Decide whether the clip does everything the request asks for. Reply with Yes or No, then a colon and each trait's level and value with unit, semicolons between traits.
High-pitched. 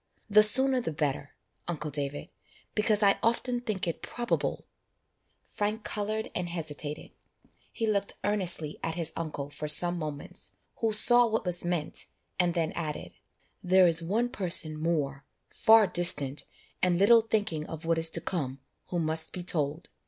No: medium, 175 Hz